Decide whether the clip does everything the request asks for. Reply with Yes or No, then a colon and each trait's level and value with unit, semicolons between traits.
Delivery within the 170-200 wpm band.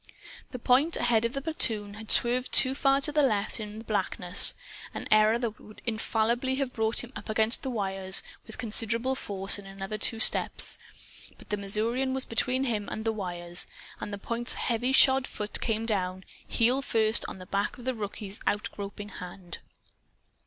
Yes: average, 185 wpm